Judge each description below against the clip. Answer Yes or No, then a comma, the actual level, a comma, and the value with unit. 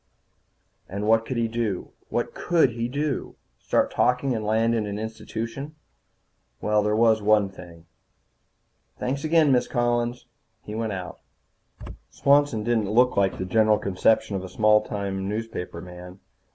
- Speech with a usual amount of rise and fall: Yes, average, 3.0 semitones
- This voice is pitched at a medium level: No, low, 110 Hz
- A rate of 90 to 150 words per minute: Yes, average, 145 wpm